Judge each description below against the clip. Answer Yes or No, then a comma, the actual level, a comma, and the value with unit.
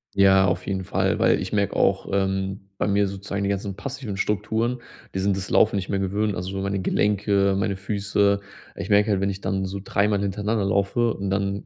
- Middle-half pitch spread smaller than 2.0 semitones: Yes, narrow, 0.9 semitones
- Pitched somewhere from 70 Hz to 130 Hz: Yes, low, 100 Hz